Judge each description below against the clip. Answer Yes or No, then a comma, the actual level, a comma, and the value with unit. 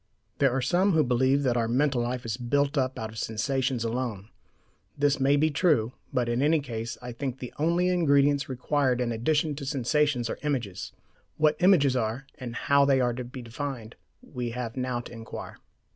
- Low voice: Yes, low, 130 Hz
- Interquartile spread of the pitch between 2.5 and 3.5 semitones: Yes, average, 3.2 semitones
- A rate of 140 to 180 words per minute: No, average, 190 wpm